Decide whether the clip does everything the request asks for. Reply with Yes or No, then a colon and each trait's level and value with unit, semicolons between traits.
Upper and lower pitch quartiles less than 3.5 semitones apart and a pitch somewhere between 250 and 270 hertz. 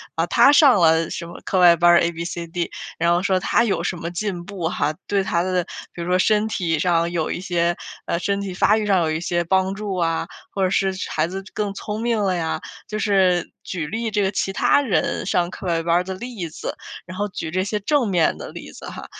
No: average, 2.9 semitones; medium, 185 Hz